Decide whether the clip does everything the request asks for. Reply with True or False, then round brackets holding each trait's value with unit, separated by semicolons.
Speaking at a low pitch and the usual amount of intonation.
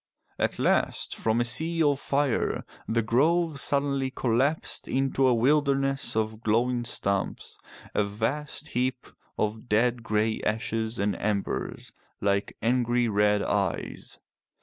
True (120 Hz; 4.0 semitones)